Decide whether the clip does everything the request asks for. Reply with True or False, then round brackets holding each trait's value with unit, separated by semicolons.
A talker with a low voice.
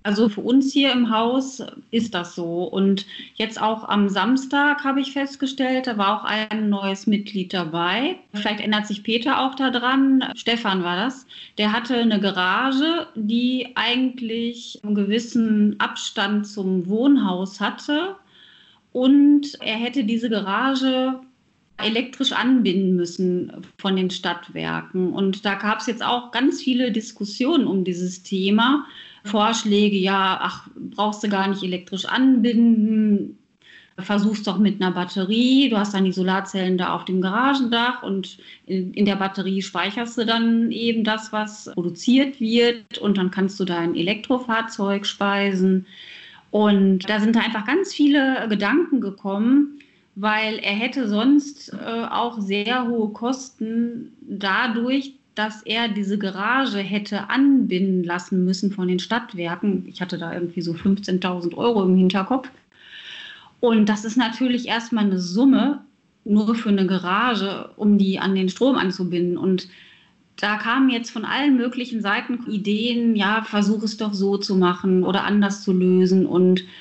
False (215 Hz)